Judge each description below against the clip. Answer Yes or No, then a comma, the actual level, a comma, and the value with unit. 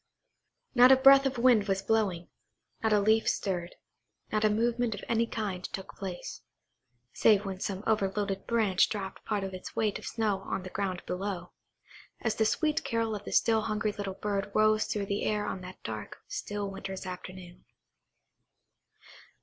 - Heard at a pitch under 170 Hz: No, high, 205 Hz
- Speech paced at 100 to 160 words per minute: No, average, 170 wpm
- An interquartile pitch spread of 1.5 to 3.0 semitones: Yes, narrow, 2.5 semitones